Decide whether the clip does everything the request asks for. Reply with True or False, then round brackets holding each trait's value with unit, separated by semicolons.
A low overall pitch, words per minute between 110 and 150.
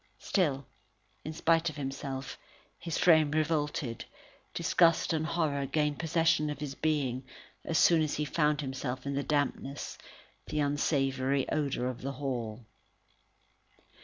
False (145 Hz; 135 wpm)